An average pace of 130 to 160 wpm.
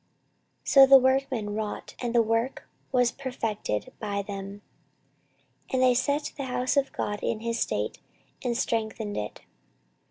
Yes: average, 150 wpm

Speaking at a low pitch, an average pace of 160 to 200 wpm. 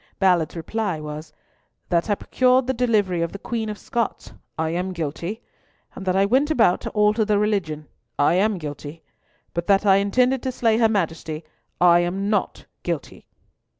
No: high, 195 Hz; average, 175 wpm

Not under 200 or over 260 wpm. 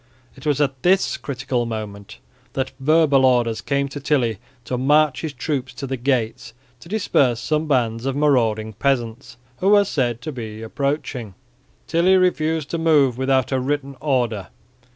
No: average, 160 wpm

